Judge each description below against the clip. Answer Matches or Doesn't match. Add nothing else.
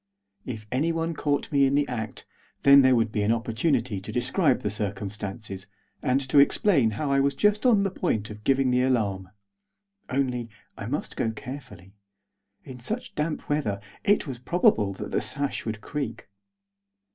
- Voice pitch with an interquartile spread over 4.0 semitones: Matches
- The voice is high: Doesn't match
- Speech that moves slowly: Doesn't match